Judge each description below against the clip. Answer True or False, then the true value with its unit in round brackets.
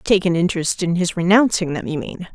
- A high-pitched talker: False (175 Hz)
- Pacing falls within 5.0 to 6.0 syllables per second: True (5.8 syllables/s)